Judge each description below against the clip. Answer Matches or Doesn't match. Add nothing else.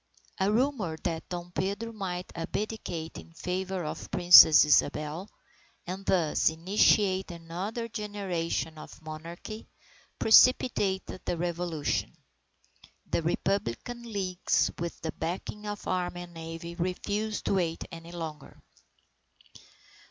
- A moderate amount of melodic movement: Matches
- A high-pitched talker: Doesn't match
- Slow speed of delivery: Matches